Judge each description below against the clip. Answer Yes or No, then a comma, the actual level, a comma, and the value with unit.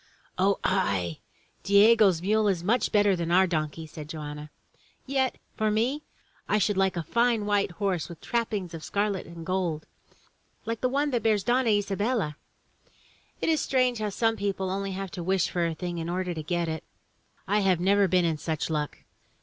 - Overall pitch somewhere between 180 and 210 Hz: Yes, high, 190 Hz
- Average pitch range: Yes, average, 4.1 semitones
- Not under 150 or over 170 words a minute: No, average, 185 wpm